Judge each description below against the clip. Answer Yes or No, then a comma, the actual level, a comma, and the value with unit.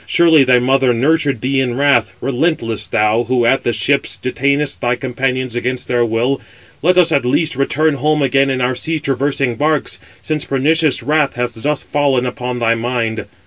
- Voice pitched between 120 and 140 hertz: Yes, low, 135 Hz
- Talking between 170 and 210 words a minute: Yes, average, 180 wpm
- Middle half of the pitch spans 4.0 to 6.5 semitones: No, average, 3.0 semitones